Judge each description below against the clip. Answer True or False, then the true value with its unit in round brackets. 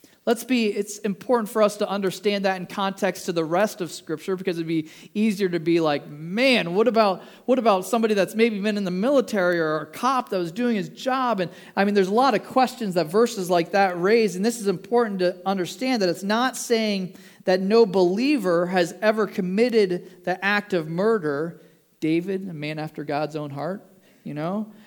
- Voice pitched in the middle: False (195 Hz)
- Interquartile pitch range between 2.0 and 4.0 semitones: True (3.7 semitones)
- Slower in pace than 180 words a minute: False (205 wpm)